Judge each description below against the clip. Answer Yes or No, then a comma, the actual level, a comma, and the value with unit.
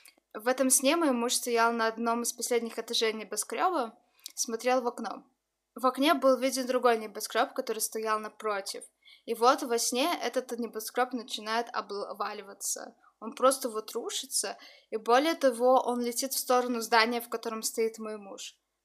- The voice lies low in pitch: No, high, 240 Hz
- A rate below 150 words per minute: No, average, 155 wpm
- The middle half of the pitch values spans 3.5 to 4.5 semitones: No, narrow, 2.6 semitones